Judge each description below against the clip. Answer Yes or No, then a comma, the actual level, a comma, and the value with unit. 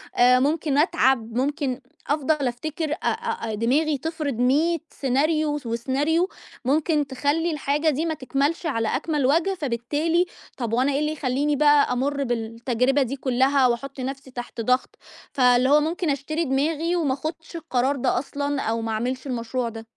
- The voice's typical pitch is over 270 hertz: Yes, very high, 280 Hz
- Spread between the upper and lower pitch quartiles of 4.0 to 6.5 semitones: No, average, 3.5 semitones